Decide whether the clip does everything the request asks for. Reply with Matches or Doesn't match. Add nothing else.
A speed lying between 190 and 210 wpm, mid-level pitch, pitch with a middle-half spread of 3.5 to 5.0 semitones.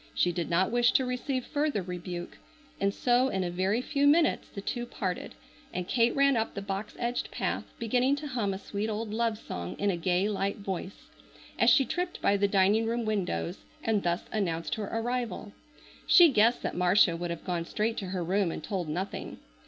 Doesn't match